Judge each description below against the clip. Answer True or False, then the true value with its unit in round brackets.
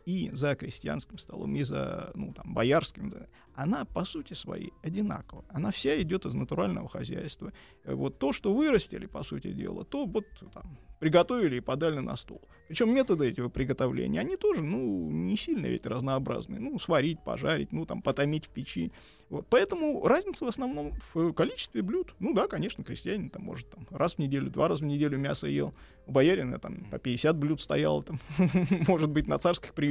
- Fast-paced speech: True (180 wpm)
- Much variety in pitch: True (6.2 semitones)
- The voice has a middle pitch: True (160 Hz)